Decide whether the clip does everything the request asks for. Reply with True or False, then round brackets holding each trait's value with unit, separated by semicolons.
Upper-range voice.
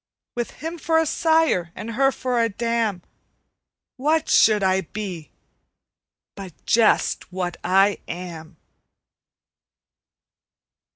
True (215 Hz)